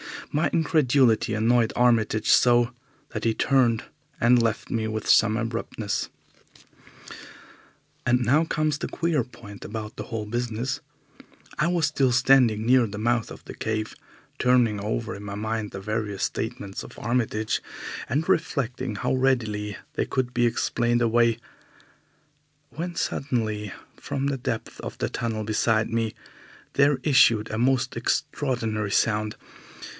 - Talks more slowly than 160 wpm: Yes, average, 140 wpm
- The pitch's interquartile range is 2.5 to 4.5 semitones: Yes, average, 2.9 semitones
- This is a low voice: Yes, low, 115 Hz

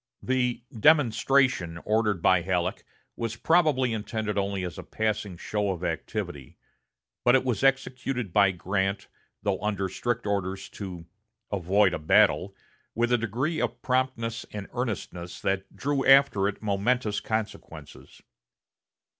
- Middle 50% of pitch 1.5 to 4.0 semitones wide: No, average, 4.4 semitones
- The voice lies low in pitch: Yes, low, 105 Hz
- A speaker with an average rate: No, slow, 130 wpm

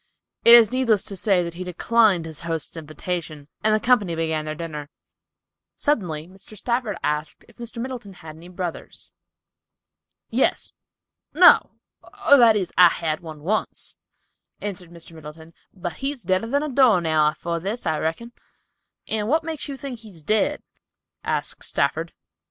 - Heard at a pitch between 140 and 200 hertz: Yes, medium, 185 Hz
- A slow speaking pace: No, average, 155 wpm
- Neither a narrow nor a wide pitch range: No, wide, 6.3 semitones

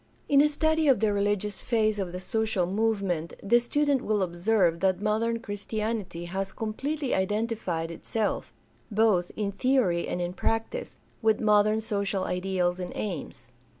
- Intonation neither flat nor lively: Yes, average, 3.5 semitones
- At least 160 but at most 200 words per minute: No, average, 150 wpm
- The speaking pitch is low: No, high, 210 Hz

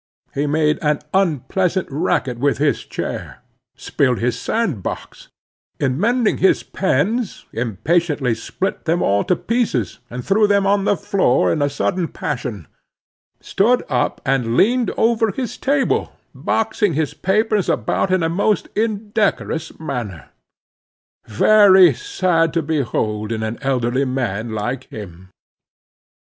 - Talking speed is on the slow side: Yes, slow, 130 wpm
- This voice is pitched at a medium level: Yes, medium, 160 Hz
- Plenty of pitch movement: Yes, wide, 8.3 semitones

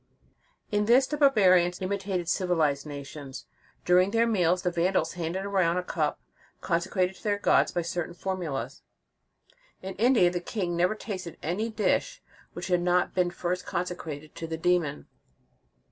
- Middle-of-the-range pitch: Yes, medium, 180 Hz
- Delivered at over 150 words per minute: Yes, average, 160 wpm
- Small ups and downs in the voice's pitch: Yes, narrow, 2.3 semitones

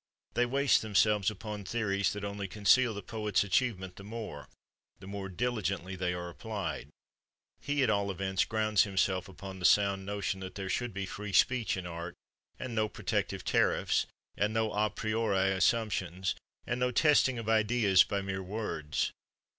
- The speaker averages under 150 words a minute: No, average, 165 wpm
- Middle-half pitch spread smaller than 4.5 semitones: Yes, average, 2.7 semitones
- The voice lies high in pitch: No, low, 100 Hz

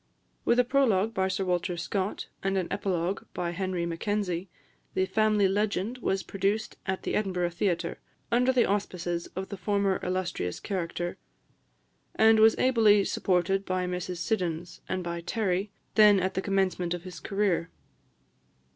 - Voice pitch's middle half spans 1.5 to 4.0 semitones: Yes, narrow, 2.6 semitones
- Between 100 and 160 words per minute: Yes, average, 150 wpm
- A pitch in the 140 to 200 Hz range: Yes, high, 190 Hz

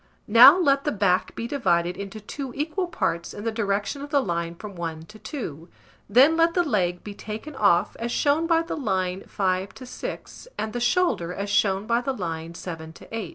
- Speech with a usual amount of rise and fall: No, wide, 7.3 semitones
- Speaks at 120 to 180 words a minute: No, fast, 205 wpm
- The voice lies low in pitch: No, high, 210 Hz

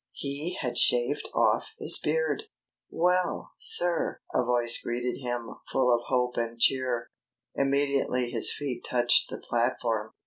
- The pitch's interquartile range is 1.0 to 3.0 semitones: Yes, average, 2.7 semitones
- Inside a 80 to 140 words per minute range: Yes, slow, 135 wpm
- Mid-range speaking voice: No, low, 125 Hz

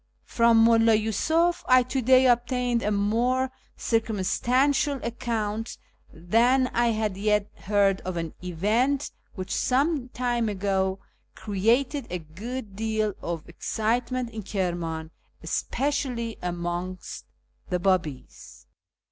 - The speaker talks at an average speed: No, slow, 115 wpm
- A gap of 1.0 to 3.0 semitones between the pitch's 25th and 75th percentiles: No, average, 4.6 semitones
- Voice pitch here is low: No, high, 225 Hz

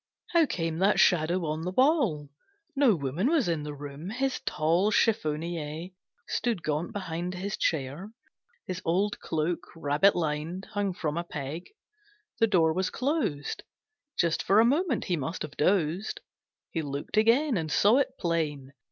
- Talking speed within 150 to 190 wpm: Yes, average, 155 wpm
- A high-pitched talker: No, medium, 175 Hz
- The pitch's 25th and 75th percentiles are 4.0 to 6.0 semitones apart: Yes, average, 5.2 semitones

